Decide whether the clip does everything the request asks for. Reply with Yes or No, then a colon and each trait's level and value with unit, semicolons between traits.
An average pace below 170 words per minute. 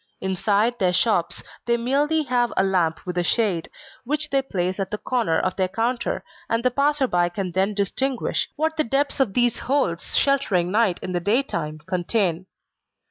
No: average, 180 wpm